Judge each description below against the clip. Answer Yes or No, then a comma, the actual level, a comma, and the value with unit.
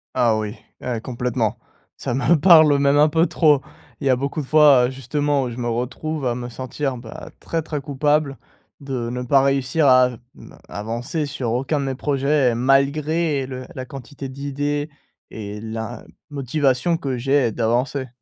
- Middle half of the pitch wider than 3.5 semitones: No, average, 2.9 semitones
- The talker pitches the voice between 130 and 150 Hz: Yes, low, 135 Hz